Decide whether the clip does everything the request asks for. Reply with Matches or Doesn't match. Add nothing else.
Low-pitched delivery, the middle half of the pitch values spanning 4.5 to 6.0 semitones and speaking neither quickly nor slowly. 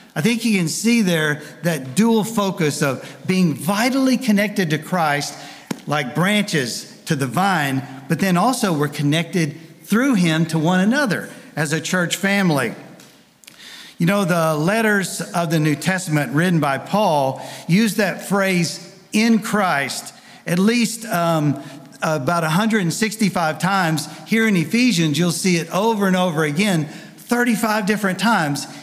Doesn't match